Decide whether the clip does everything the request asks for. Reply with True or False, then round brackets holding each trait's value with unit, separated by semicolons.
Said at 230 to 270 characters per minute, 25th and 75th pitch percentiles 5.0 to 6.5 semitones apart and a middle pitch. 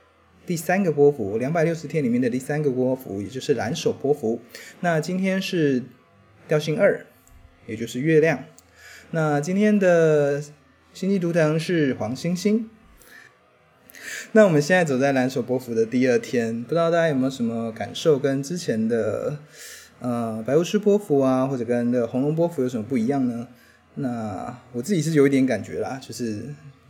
True (255 characters per minute; 5.4 semitones; 145 Hz)